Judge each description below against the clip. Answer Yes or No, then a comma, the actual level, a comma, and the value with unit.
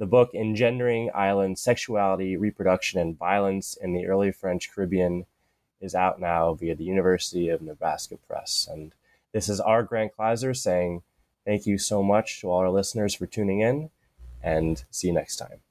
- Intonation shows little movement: No, average, 3.1 semitones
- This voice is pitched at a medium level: No, very low, 95 Hz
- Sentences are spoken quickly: No, average, 170 wpm